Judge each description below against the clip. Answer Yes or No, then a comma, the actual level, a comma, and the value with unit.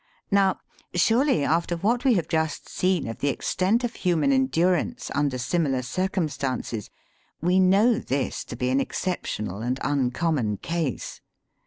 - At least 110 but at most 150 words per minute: Yes, average, 140 wpm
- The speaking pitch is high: No, medium, 165 Hz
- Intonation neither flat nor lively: No, wide, 6.1 semitones